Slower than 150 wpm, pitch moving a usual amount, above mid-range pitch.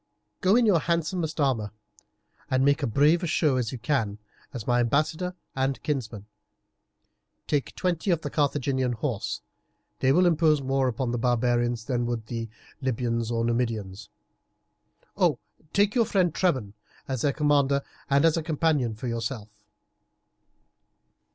No: average, 140 wpm; average, 4.8 semitones; low, 135 Hz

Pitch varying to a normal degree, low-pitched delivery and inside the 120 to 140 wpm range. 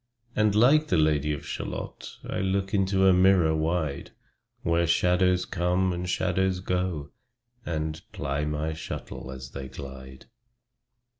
Yes: average, 3.7 semitones; very low, 85 Hz; slow, 135 wpm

